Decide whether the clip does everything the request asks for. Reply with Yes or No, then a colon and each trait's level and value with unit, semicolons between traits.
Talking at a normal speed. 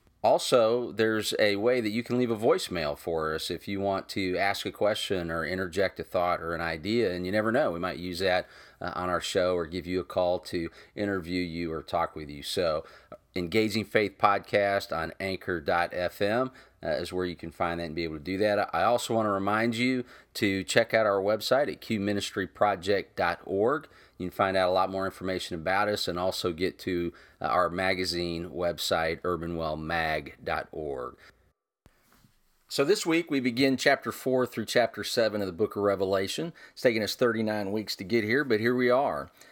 Yes: average, 190 wpm